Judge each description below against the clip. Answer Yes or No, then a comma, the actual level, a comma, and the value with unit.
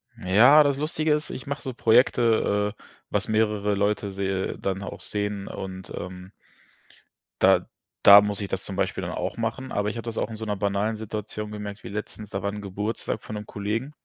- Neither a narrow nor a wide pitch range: No, narrow, 2.0 semitones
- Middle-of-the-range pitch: No, low, 105 Hz